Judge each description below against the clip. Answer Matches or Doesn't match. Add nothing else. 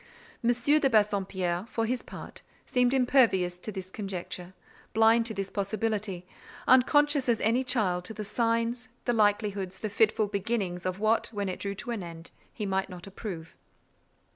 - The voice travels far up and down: Doesn't match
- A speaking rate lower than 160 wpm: Doesn't match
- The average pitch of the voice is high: Matches